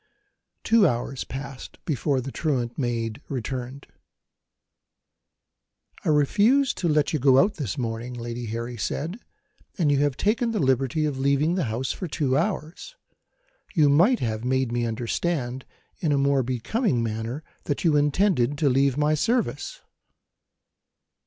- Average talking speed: Yes, average, 145 wpm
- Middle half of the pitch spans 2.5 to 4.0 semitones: No, average, 4.5 semitones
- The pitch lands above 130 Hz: Yes, medium, 140 Hz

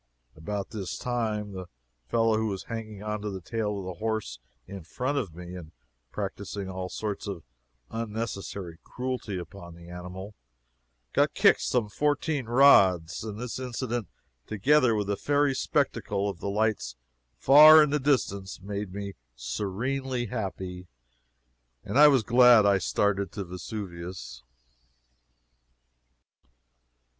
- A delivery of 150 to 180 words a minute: No, slow, 135 wpm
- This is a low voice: Yes, low, 105 Hz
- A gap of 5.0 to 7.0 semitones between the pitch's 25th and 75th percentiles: No, average, 4.3 semitones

